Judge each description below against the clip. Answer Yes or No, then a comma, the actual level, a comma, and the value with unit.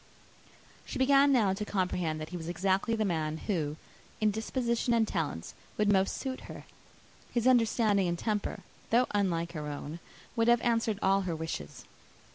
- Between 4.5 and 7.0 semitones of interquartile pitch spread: Yes, average, 5.3 semitones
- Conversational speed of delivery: Yes, average, 165 wpm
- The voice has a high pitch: Yes, high, 200 Hz